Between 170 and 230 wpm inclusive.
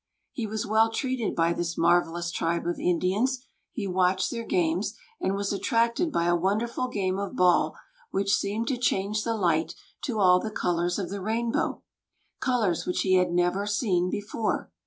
Yes: average, 175 wpm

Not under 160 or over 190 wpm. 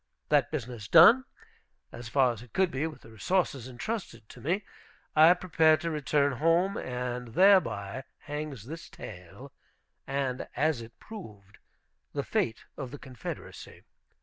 No: average, 145 wpm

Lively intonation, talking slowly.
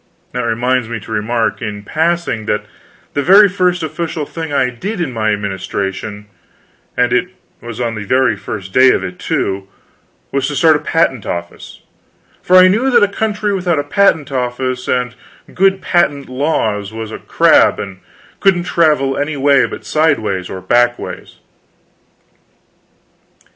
No: wide, 7.2 semitones; average, 160 wpm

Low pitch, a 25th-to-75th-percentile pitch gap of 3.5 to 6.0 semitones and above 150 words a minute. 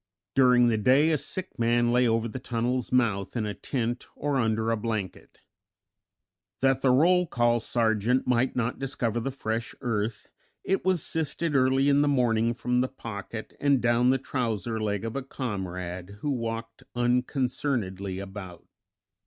No: low, 120 Hz; average, 3.0 semitones; average, 160 wpm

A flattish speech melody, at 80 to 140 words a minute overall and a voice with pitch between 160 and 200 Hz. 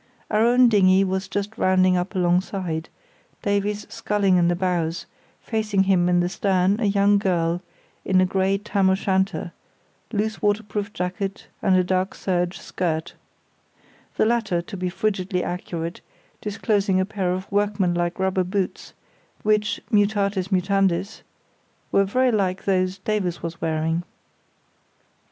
Yes: narrow, 2.2 semitones; slow, 135 wpm; high, 190 Hz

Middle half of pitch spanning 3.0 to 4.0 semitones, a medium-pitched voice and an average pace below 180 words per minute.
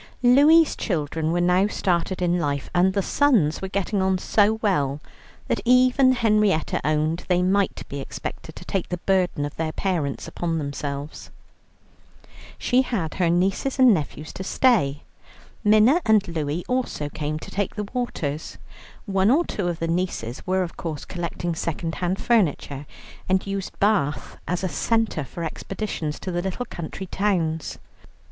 No: average, 4.8 semitones; medium, 180 Hz; average, 160 wpm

